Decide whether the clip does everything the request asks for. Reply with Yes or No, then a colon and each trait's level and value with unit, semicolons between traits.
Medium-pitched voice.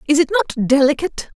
No: very high, 290 Hz